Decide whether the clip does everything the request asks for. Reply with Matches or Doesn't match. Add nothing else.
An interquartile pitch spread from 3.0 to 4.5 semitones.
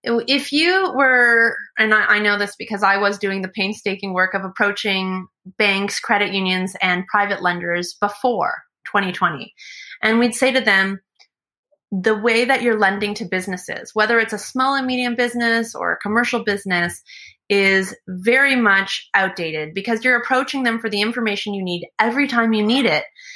Matches